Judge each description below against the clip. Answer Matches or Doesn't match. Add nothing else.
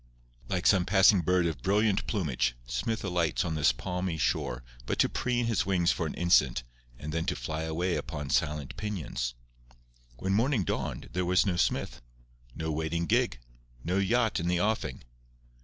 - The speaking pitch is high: Doesn't match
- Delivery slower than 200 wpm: Matches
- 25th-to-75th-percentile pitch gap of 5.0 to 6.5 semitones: Doesn't match